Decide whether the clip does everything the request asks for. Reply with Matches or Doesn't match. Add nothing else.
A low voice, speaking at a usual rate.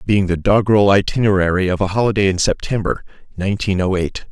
Matches